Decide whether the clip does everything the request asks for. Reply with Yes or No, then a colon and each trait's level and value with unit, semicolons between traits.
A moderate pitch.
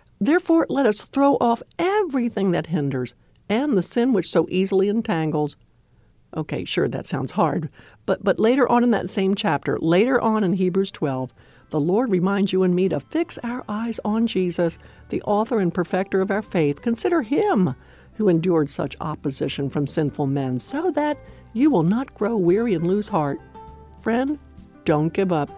No: high, 195 Hz